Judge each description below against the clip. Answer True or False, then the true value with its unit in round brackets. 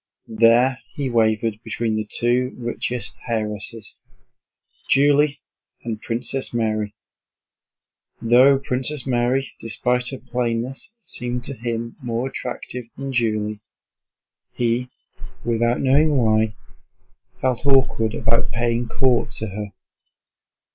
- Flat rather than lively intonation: True (2.2 semitones)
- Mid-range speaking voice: False (120 Hz)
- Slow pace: True (105 wpm)